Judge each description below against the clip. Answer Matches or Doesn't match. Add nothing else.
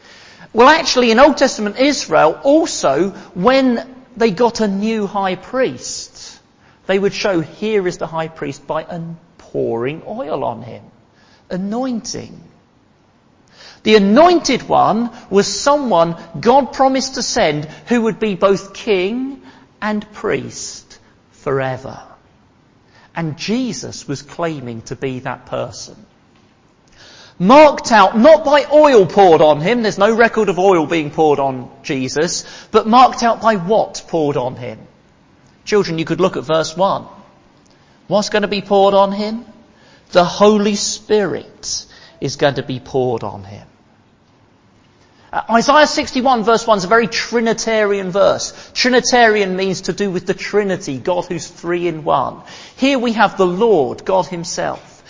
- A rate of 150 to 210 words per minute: Doesn't match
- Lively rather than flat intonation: Matches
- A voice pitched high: Matches